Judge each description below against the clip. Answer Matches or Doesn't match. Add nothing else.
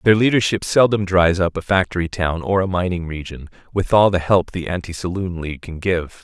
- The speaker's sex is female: Doesn't match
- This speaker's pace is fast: Matches